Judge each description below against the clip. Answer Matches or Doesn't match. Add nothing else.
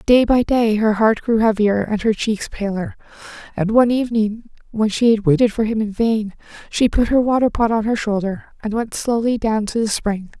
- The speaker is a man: Doesn't match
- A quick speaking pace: Matches